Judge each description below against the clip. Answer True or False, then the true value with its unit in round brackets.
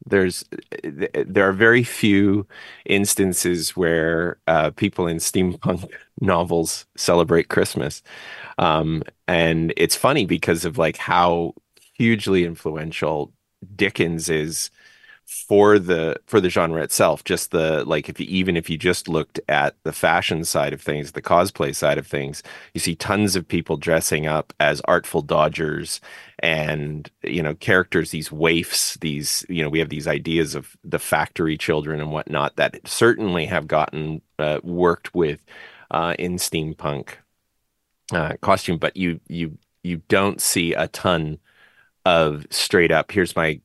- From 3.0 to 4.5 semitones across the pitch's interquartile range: False (2.4 semitones)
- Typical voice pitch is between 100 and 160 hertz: False (85 Hz)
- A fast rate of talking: False (145 wpm)